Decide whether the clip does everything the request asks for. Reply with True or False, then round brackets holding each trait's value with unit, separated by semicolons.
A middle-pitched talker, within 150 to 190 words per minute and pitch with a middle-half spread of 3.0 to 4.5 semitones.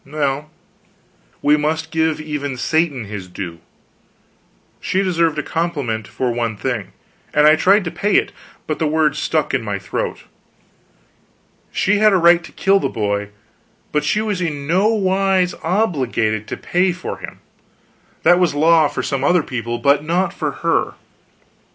False (155 Hz; 160 wpm; 5.3 semitones)